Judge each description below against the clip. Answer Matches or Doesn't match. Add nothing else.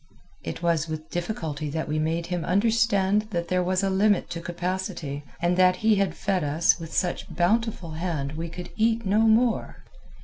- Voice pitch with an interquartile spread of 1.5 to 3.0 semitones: Doesn't match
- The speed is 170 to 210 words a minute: Matches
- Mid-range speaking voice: Matches